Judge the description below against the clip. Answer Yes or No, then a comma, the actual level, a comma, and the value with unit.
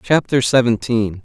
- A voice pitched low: Yes, low, 120 Hz